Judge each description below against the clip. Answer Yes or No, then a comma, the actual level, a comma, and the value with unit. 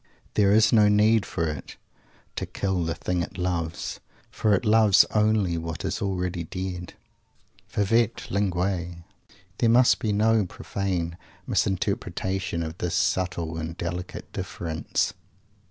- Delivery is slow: Yes, slow, 130 wpm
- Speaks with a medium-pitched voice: No, very low, 95 Hz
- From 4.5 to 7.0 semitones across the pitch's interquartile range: No, average, 3.2 semitones